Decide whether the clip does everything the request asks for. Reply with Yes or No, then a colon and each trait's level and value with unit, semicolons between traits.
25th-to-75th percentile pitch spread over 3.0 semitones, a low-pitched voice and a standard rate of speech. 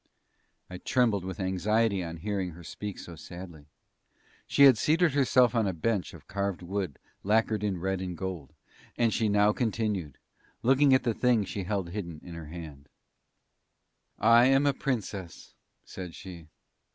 Yes: average, 4.5 semitones; low, 100 Hz; average, 160 wpm